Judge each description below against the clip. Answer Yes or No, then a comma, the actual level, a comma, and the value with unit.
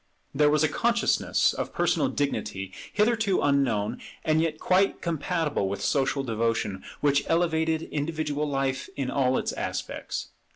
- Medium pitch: Yes, medium, 145 Hz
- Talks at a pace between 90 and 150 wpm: Yes, slow, 135 wpm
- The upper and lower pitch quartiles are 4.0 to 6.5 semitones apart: No, average, 3.6 semitones